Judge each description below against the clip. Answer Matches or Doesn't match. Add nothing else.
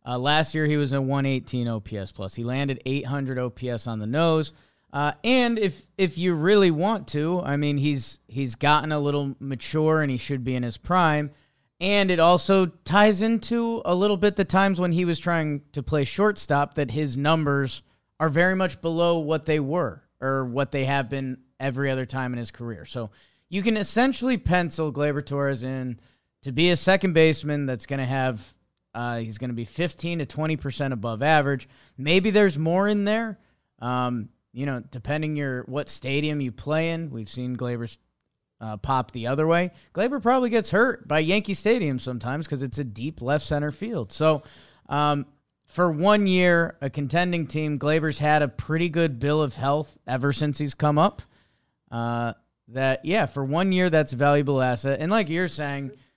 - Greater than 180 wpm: Matches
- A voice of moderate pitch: Matches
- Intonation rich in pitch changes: Doesn't match